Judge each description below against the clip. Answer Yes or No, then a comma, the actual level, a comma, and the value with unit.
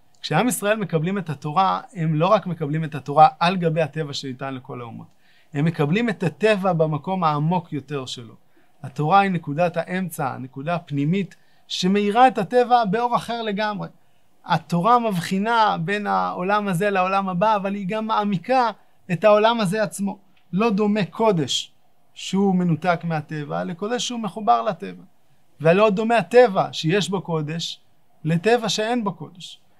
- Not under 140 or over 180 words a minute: Yes, average, 145 wpm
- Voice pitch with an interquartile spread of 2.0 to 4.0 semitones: No, average, 5.1 semitones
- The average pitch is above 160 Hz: Yes, medium, 185 Hz